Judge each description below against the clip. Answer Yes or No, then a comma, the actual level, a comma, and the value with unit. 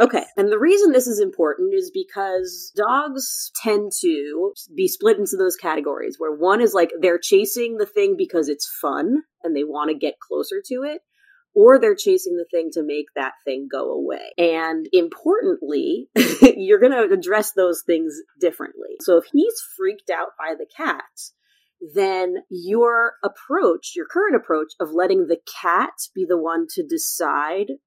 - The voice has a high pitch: Yes, very high, 255 Hz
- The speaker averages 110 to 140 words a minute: No, average, 170 wpm